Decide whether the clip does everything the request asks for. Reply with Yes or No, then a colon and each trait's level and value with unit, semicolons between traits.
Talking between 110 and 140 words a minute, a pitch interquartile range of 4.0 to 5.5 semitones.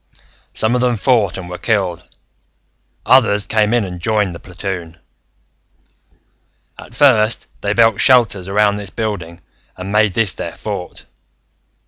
No: slow, 135 wpm; average, 3.5 semitones